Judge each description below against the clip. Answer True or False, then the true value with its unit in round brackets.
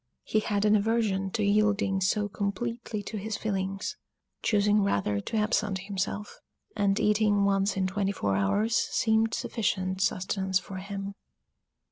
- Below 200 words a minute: True (140 wpm)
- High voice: True (200 Hz)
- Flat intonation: True (1.7 semitones)